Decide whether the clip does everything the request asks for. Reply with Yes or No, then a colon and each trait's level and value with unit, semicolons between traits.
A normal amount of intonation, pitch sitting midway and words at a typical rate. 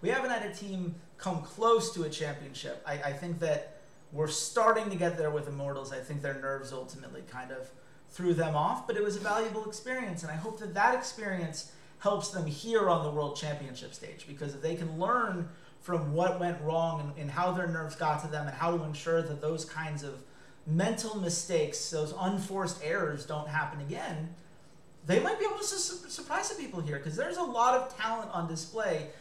No: average, 4.9 semitones; medium, 165 Hz; fast, 210 wpm